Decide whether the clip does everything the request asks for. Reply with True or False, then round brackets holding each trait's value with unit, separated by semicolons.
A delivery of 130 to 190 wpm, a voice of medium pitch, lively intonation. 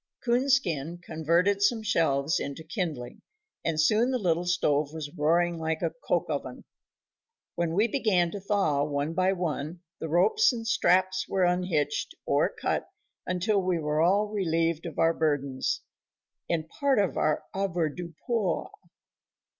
False (140 wpm; 175 Hz; 3.9 semitones)